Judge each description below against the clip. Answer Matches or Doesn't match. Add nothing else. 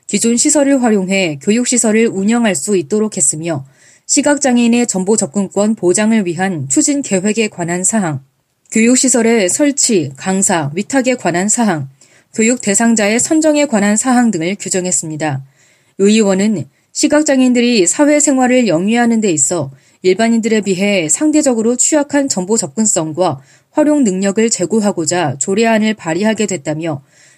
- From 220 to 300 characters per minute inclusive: Doesn't match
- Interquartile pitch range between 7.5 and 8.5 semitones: Doesn't match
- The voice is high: Matches